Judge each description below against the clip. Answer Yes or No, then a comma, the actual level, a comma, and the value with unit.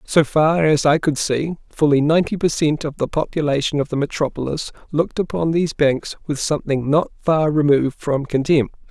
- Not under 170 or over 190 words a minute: Yes, average, 180 wpm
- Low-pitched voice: No, medium, 150 Hz